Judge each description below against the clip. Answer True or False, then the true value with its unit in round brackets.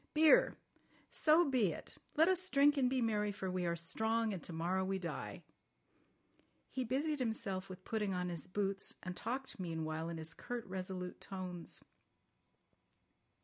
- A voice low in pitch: False (195 Hz)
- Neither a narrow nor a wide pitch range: False (6.0 semitones)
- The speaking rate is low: False (155 wpm)